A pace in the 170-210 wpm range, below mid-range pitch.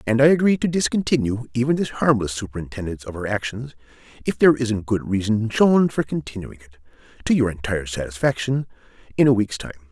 Yes: average, 175 wpm; low, 115 Hz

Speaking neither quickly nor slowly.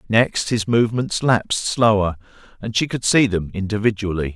Yes: average, 150 wpm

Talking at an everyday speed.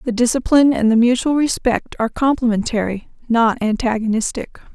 No: slow, 125 wpm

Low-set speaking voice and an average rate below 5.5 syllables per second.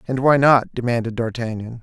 No: low, 120 Hz; 5.7 syllables/s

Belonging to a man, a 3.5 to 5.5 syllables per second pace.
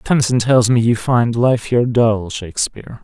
Yes: male; 5.0 syllables/s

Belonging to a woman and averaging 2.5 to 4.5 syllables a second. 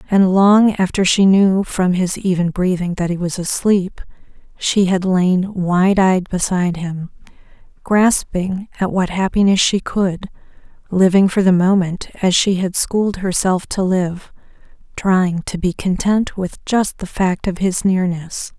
Yes: female; 4.1 syllables/s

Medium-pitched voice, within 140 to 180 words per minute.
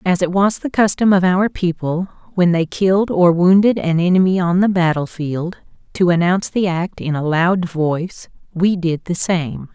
No: medium, 180 Hz; average, 190 wpm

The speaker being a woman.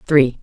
Yes: female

